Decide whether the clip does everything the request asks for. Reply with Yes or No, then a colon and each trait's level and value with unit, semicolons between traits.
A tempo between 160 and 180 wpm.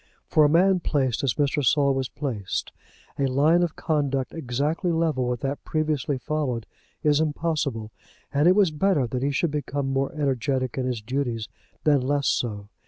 Yes: average, 170 wpm